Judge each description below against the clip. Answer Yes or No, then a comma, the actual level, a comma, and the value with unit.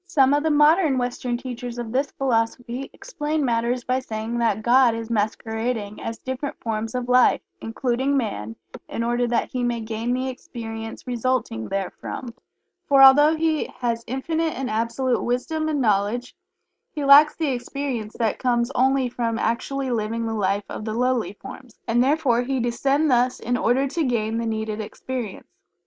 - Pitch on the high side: Yes, high, 245 Hz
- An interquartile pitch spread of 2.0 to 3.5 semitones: Yes, average, 2.9 semitones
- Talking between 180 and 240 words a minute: No, average, 165 wpm